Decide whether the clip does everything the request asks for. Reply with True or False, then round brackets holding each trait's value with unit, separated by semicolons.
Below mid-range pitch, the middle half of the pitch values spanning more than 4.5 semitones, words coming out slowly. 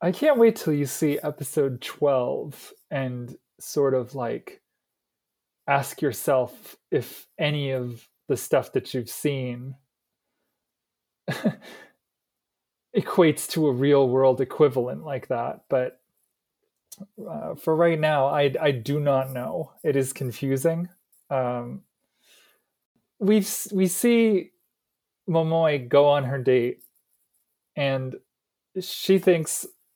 False (145 Hz; 5.2 semitones; 110 wpm)